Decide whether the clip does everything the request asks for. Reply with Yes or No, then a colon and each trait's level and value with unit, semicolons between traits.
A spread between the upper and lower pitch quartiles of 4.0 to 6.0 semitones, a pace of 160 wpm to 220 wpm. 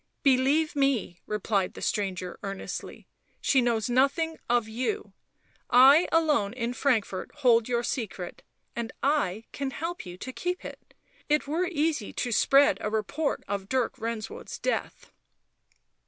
No: average, 5.3 semitones; average, 150 wpm